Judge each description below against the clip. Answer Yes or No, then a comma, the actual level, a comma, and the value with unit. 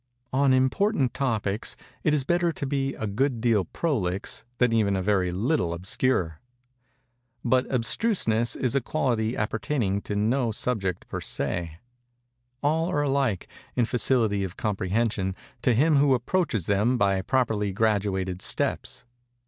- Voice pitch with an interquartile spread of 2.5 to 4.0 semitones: No, average, 5.3 semitones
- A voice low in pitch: Yes, low, 115 Hz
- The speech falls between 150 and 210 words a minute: No, average, 140 wpm